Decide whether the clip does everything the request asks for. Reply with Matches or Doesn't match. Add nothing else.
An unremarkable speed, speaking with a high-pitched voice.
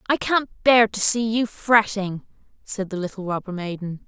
Matches